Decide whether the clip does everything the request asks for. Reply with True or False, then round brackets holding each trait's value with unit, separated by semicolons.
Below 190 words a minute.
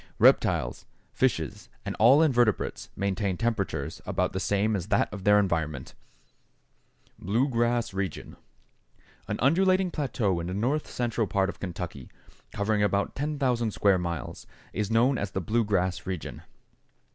True (140 wpm)